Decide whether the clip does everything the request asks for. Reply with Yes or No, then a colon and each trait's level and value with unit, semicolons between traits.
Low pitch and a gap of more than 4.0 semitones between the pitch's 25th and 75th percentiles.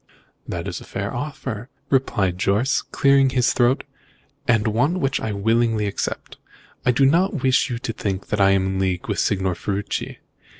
Yes: low, 115 Hz; average, 5.1 semitones